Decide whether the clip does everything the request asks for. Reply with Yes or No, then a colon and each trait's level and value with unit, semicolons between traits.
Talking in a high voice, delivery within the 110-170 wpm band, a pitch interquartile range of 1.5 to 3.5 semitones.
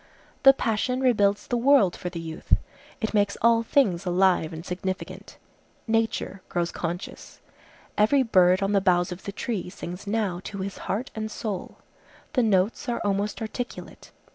No: high, 200 Hz; average, 160 wpm; average, 3.9 semitones